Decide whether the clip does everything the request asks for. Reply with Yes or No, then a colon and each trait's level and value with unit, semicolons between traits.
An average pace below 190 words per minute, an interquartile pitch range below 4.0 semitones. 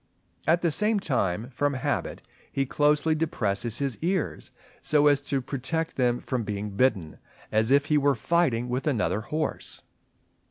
No: average, 155 wpm; average, 4.4 semitones